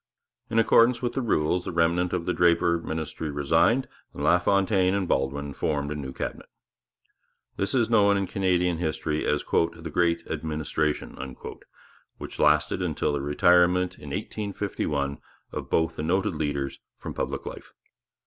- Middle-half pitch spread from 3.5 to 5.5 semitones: Yes, average, 3.8 semitones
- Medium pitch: No, very low, 85 Hz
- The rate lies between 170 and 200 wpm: No, average, 150 wpm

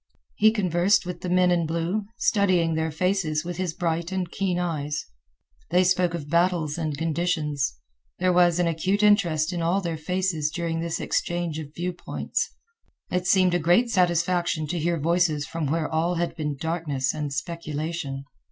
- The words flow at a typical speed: Yes, average, 170 wpm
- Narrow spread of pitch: Yes, narrow, 2.3 semitones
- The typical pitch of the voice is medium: Yes, medium, 170 Hz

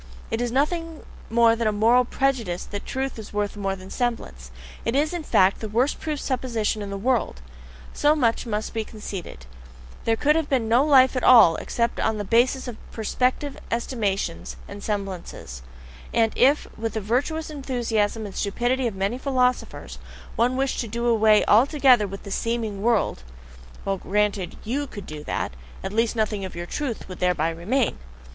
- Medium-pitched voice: No, high, 230 Hz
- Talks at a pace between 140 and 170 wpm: No, average, 180 wpm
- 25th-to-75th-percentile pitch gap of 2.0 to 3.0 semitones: No, average, 4.1 semitones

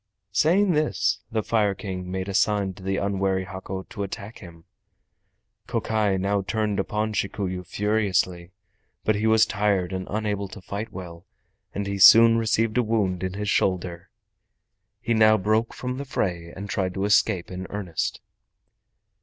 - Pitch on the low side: Yes, low, 100 Hz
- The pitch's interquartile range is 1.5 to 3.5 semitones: Yes, narrow, 2.5 semitones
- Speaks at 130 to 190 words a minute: Yes, average, 160 wpm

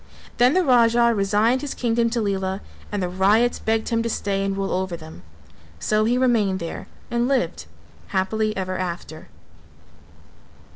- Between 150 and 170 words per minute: Yes, average, 155 wpm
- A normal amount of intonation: Yes, average, 3.8 semitones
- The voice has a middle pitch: No, high, 215 Hz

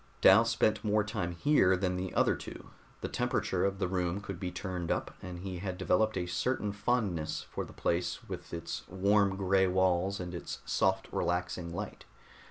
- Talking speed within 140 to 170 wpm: No, average, 180 wpm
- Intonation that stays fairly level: Yes, narrow, 2.3 semitones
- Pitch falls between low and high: No, very low, 95 Hz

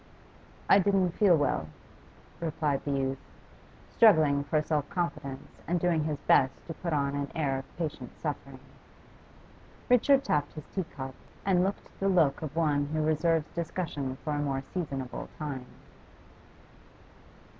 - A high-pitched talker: No, medium, 155 Hz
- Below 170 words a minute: Yes, average, 145 wpm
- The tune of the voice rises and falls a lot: No, average, 3.3 semitones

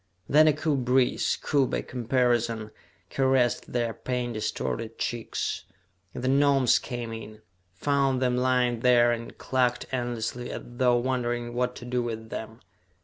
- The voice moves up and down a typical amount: No, narrow, 1.5 semitones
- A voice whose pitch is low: Yes, low, 125 Hz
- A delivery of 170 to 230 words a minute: No, average, 145 wpm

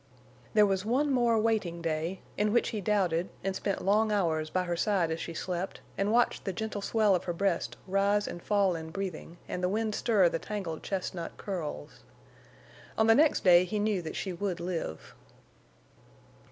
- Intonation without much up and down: No, average, 3.5 semitones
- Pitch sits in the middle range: No, high, 195 Hz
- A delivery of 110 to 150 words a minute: No, average, 185 wpm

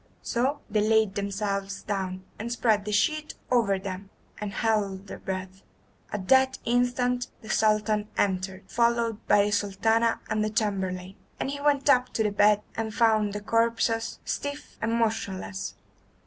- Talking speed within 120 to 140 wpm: No, average, 155 wpm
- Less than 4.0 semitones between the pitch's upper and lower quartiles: Yes, average, 2.8 semitones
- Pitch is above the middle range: Yes, high, 215 Hz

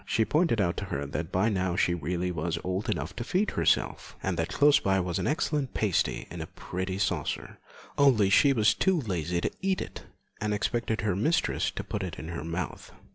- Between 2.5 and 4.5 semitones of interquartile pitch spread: No, average, 5.1 semitones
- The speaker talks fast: Yes, fast, 210 wpm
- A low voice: Yes, very low, 95 Hz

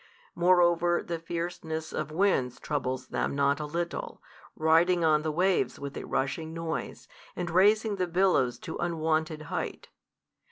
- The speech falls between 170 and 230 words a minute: No, average, 145 wpm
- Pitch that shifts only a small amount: Yes, narrow, 2.2 semitones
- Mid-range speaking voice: Yes, medium, 165 Hz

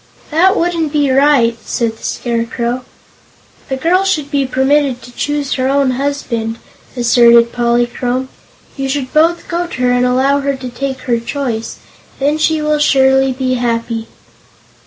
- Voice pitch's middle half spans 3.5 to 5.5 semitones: No, average, 3.1 semitones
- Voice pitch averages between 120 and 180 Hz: No, very high, 265 Hz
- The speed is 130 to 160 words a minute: Yes, average, 155 wpm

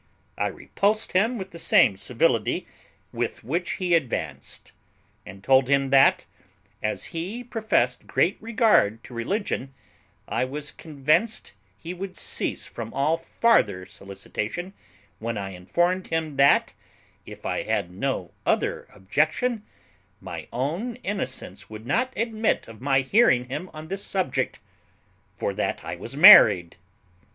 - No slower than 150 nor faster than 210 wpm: No, slow, 135 wpm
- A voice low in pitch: No, medium, 145 Hz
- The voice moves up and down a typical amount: No, wide, 8.7 semitones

